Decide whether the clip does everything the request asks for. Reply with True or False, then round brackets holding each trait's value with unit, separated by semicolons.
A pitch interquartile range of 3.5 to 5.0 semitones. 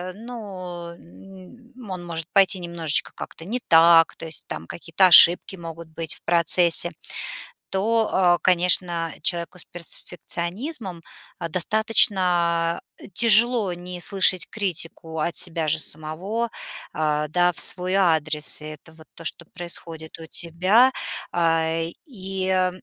False (2.7 semitones)